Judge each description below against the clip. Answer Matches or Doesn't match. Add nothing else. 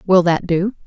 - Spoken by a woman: Matches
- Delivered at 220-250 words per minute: Doesn't match